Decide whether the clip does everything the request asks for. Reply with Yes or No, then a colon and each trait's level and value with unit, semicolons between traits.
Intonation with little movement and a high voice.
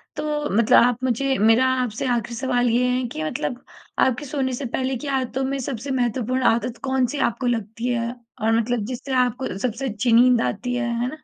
Yes: narrow, 2.0 semitones; high, 245 Hz